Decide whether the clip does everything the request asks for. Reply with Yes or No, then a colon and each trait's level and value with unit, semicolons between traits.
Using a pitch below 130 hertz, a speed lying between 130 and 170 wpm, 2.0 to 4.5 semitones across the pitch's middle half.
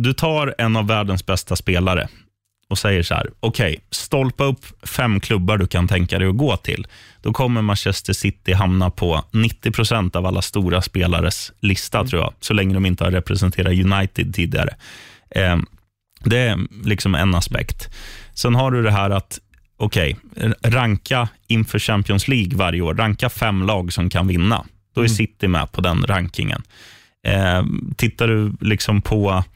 Yes: low, 100 Hz; average, 165 wpm; average, 3.4 semitones